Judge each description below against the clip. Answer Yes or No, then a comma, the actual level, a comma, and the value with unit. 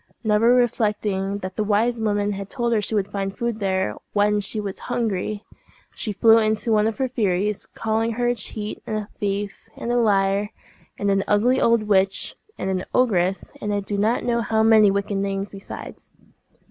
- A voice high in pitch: Yes, high, 210 Hz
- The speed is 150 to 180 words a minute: No, average, 190 wpm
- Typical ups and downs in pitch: No, narrow, 2.1 semitones